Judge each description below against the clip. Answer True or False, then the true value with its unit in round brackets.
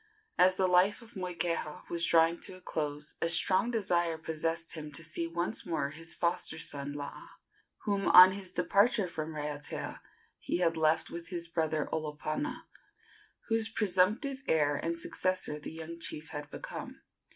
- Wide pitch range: False (3.0 semitones)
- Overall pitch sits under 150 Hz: False (170 Hz)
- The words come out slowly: False (160 wpm)